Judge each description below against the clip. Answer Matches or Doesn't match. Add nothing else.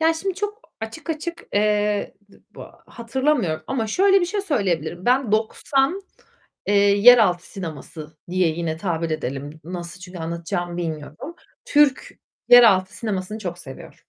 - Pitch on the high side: Matches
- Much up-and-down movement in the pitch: Matches